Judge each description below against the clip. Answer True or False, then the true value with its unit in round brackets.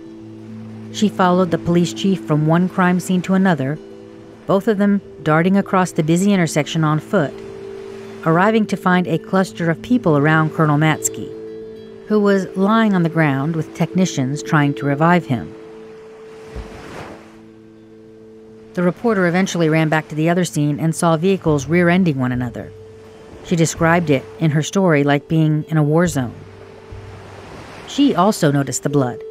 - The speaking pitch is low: False (160 Hz)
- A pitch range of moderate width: False (6.4 semitones)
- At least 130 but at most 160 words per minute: True (155 wpm)